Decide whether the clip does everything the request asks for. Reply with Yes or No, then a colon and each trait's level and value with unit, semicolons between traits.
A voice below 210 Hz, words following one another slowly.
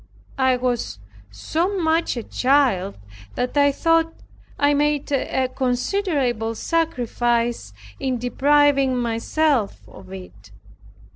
No: very high, 255 Hz; slow, 100 wpm